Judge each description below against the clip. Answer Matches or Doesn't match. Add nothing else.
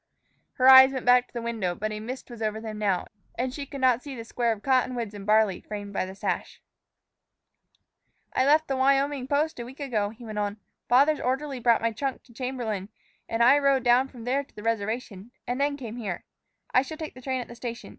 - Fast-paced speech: Matches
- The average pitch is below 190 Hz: Doesn't match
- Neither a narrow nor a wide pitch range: Matches